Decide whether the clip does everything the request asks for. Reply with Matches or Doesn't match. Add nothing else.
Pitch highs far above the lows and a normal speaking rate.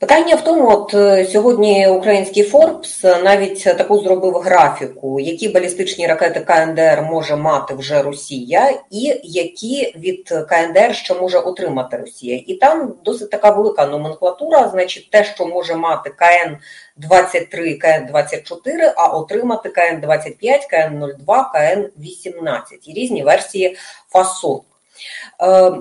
Doesn't match